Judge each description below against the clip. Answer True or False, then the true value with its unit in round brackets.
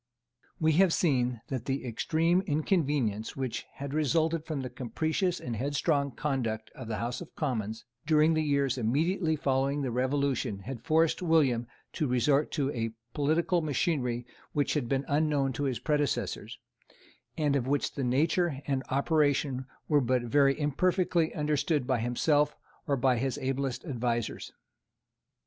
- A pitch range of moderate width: True (3.6 semitones)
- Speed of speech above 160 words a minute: False (150 wpm)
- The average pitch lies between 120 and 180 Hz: True (140 Hz)